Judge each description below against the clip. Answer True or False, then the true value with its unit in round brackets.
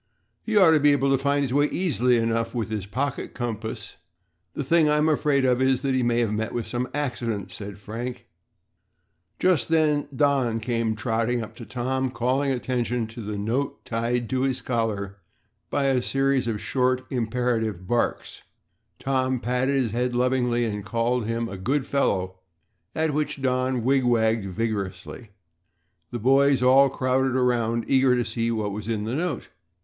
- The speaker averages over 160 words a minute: True (170 wpm)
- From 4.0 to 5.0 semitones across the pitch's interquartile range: False (2.8 semitones)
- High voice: False (125 Hz)